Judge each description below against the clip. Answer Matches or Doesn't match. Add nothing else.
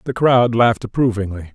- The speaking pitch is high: Doesn't match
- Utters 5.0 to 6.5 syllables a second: Matches